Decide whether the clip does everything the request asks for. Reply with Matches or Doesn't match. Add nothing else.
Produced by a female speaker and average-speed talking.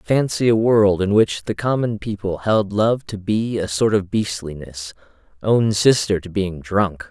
Doesn't match